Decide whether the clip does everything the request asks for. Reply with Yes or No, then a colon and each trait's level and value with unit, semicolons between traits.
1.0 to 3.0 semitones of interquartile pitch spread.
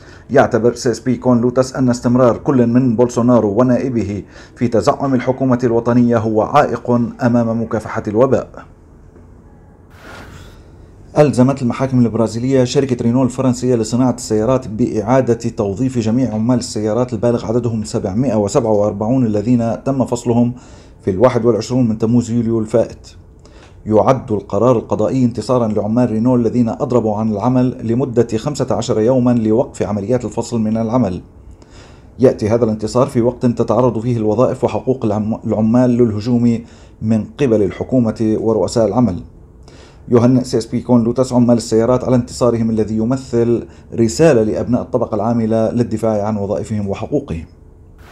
Yes: narrow, 2.4 semitones